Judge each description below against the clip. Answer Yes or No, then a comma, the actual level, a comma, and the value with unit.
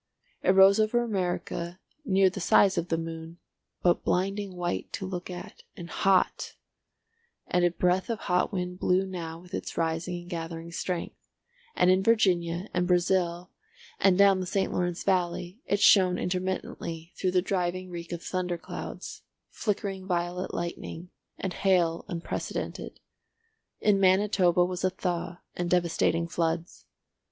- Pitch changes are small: Yes, narrow, 1.6 semitones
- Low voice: No, medium, 180 Hz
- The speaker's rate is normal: Yes, average, 145 wpm